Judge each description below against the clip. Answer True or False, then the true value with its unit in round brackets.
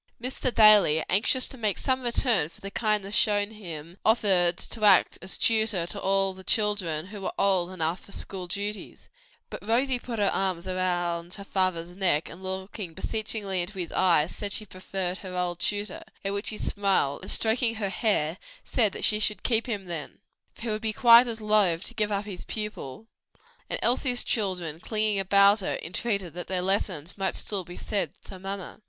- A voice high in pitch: True (195 Hz)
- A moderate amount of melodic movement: True (3.0 semitones)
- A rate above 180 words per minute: True (190 wpm)